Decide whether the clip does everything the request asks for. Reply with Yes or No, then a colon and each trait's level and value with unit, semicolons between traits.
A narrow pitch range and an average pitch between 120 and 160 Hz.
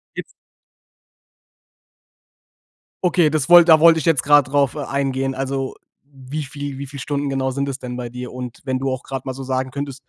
Yes: narrow, 1.7 semitones; low, 135 Hz